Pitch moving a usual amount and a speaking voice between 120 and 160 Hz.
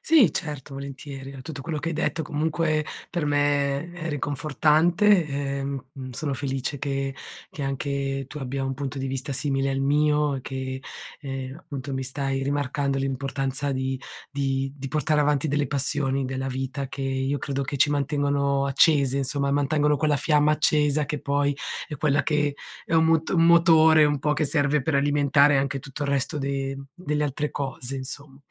No: narrow, 1.7 semitones; medium, 140 Hz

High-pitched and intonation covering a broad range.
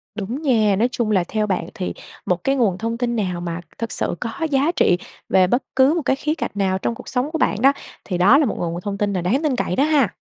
Yes: high, 225 Hz; wide, 6.0 semitones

